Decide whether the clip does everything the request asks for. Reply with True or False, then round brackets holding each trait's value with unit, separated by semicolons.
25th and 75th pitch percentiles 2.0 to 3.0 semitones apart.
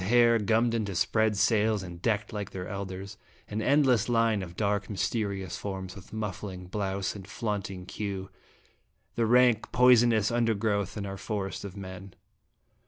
True (2.7 semitones)